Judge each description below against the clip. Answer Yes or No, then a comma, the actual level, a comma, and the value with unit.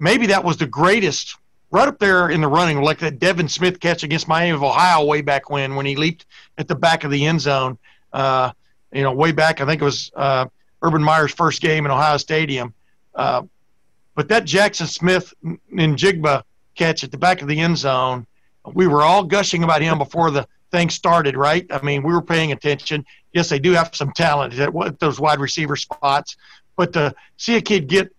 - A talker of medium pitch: Yes, medium, 155 Hz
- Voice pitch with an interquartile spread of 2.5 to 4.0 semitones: Yes, average, 3.3 semitones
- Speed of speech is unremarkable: No, fast, 210 wpm